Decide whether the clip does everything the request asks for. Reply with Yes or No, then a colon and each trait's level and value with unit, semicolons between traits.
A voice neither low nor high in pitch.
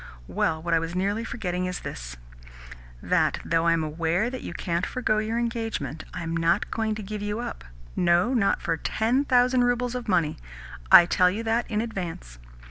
No: high, 195 Hz